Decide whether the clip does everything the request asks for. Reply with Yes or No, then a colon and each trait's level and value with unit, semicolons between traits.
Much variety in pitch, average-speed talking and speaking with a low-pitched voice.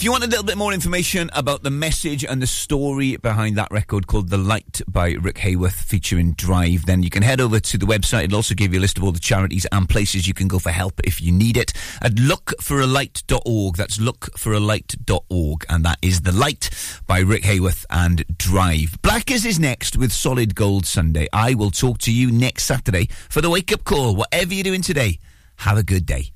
No: wide, 6.0 semitones; fast, 215 wpm; low, 105 Hz